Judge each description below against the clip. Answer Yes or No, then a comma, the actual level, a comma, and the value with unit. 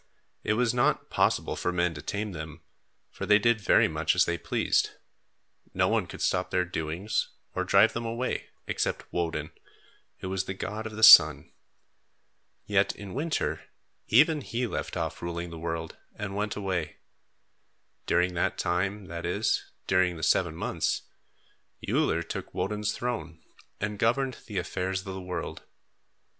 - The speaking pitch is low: Yes, very low, 95 Hz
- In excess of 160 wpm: No, average, 155 wpm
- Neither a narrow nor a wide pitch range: Yes, average, 4.1 semitones